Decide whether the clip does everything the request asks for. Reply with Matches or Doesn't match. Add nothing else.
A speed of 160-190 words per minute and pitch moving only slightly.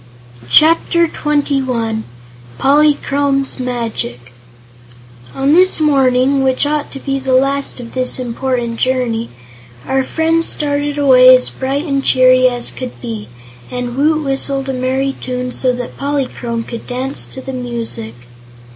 Doesn't match